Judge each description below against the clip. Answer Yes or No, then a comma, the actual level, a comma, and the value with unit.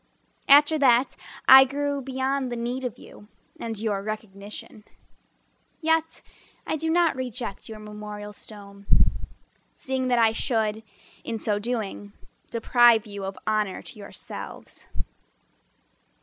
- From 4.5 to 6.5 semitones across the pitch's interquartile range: No, average, 4.0 semitones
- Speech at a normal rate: No, slow, 120 wpm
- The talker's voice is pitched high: Yes, high, 230 Hz